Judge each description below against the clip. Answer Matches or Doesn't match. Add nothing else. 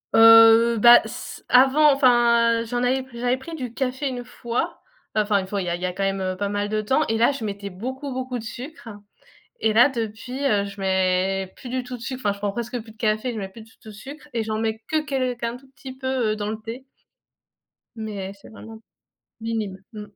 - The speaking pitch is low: Doesn't match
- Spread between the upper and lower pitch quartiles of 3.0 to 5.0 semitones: Matches